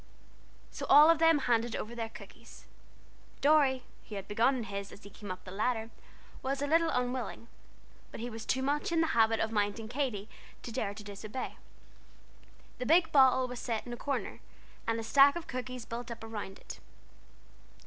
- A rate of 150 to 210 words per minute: Yes, average, 190 wpm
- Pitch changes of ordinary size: Yes, average, 3.8 semitones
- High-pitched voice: Yes, high, 240 Hz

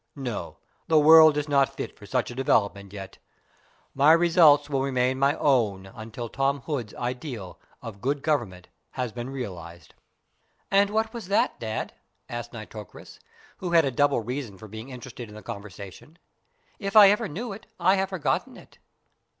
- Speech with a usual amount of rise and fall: No, wide, 6.3 semitones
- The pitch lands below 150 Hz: Yes, low, 135 Hz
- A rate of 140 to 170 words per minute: Yes, average, 165 wpm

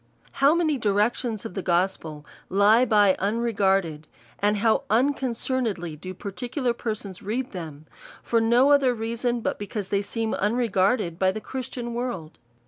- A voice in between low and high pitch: No, high, 215 Hz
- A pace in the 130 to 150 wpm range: Yes, average, 145 wpm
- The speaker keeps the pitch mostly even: No, average, 4.1 semitones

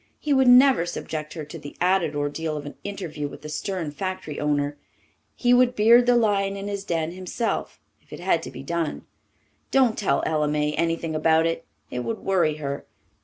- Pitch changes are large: No, average, 5.0 semitones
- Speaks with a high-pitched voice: No, medium, 170 Hz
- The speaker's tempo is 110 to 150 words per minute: No, average, 195 wpm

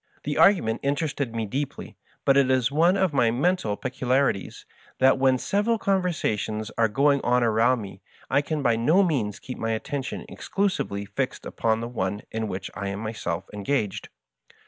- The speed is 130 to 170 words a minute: No, average, 180 wpm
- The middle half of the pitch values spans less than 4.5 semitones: No, average, 4.8 semitones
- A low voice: Yes, low, 125 Hz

